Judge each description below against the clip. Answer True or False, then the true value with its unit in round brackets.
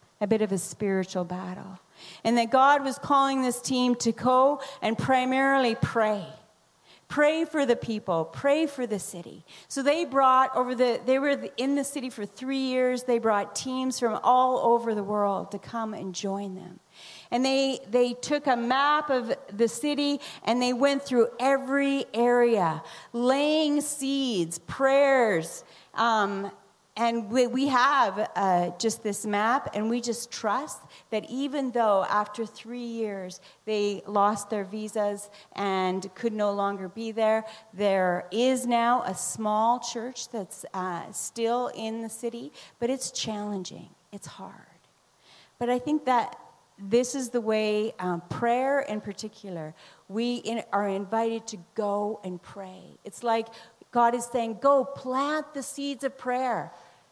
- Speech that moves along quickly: False (155 wpm)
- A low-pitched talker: False (230 Hz)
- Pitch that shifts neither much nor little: True (4.1 semitones)